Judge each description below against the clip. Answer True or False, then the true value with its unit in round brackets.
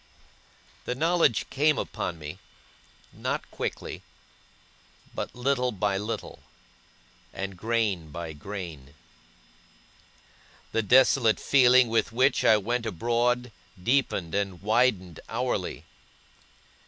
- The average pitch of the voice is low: True (115 Hz)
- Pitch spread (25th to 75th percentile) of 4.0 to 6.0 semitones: True (4.7 semitones)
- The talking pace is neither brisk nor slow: False (95 wpm)